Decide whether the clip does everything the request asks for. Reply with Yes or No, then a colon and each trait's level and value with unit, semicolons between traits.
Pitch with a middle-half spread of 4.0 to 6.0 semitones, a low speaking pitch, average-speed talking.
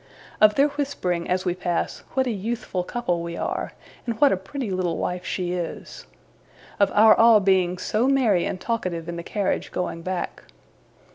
No: average, 4.5 semitones; high, 190 Hz; average, 180 wpm